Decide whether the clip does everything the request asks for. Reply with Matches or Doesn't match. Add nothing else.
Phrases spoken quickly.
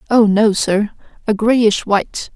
Doesn't match